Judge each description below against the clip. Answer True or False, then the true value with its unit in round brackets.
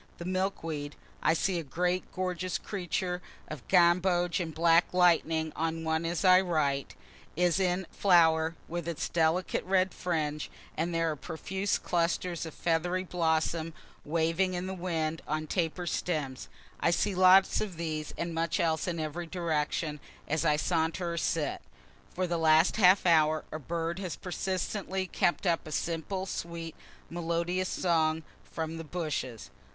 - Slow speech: False (155 wpm)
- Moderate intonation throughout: False (2.2 semitones)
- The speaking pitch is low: False (170 Hz)